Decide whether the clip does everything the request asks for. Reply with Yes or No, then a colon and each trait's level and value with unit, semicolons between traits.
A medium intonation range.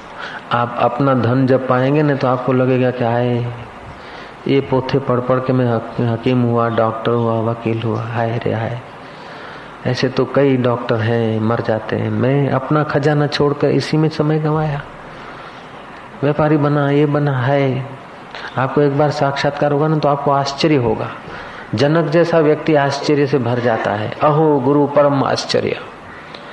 Yes: average, 3.5 semitones